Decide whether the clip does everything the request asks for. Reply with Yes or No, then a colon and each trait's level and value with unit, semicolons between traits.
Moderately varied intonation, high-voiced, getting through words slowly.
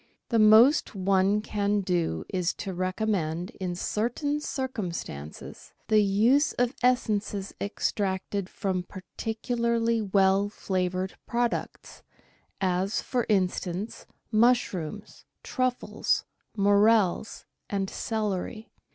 Yes: average, 3.3 semitones; high, 205 Hz; slow, 95 wpm